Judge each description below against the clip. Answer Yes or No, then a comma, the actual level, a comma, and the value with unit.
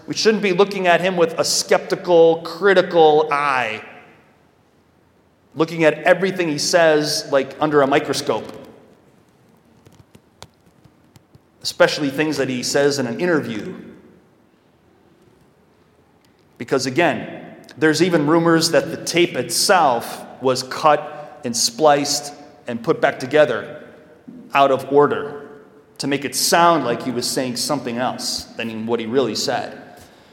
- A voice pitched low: No, medium, 150 Hz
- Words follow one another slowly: Yes, slow, 125 wpm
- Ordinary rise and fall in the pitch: Yes, average, 3.6 semitones